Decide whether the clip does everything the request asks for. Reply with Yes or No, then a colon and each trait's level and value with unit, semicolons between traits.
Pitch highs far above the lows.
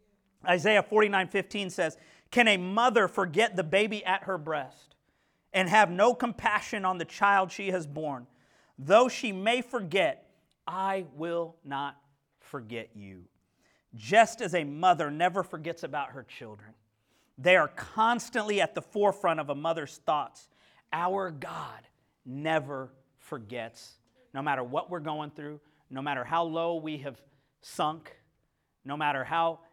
Yes: wide, 5.7 semitones